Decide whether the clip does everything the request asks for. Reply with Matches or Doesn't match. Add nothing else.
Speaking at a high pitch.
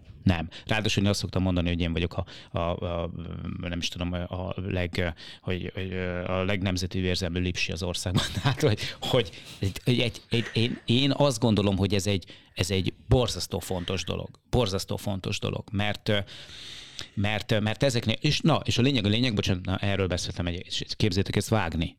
Doesn't match